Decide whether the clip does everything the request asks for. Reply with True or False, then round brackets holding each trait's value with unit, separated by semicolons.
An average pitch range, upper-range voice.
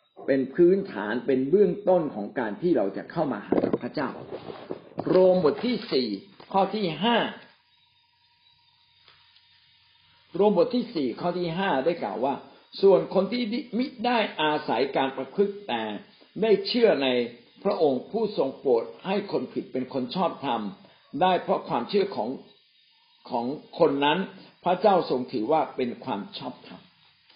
False (6.9 semitones; 195 Hz)